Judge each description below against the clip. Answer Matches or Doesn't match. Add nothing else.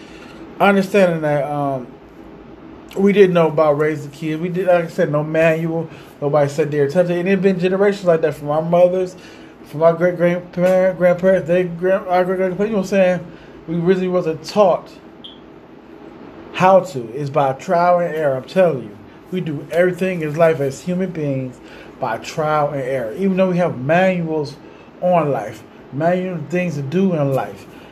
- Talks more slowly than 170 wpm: Doesn't match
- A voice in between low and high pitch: Matches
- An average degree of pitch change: Matches